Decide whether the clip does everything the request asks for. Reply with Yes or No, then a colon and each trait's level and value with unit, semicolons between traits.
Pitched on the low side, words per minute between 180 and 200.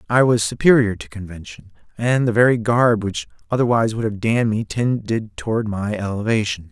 No: low, 110 Hz; average, 170 wpm